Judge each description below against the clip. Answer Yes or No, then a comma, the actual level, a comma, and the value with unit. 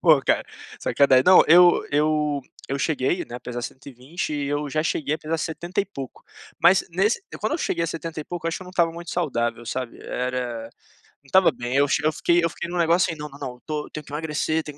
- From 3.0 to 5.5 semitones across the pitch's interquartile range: Yes, average, 3.7 semitones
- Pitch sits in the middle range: Yes, medium, 155 Hz